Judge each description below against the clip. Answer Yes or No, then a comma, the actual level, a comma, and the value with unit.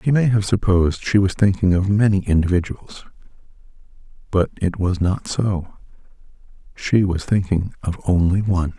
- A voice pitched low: Yes, very low, 95 Hz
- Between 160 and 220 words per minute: No, slow, 135 wpm